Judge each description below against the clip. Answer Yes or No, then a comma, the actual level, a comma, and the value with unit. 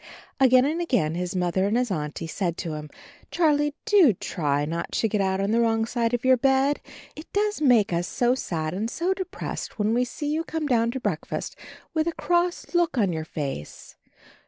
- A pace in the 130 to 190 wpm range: No, fast, 205 wpm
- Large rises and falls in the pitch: Yes, wide, 8.6 semitones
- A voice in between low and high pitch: No, high, 235 Hz